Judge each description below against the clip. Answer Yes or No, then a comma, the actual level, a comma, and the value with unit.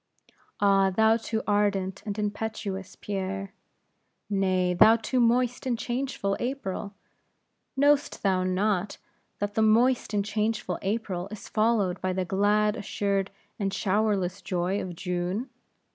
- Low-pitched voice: No, high, 205 Hz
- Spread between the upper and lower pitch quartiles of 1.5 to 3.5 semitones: Yes, narrow, 2.5 semitones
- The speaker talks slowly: Yes, slow, 130 wpm